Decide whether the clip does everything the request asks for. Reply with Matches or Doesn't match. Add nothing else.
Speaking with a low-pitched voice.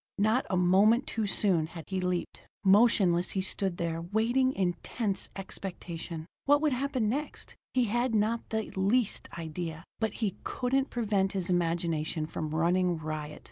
Doesn't match